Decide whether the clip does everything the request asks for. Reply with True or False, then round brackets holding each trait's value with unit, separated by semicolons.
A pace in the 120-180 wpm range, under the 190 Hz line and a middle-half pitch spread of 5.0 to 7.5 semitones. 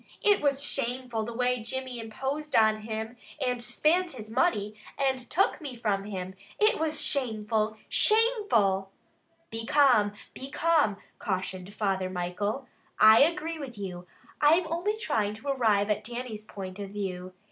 False (150 wpm; 230 Hz; 5.3 semitones)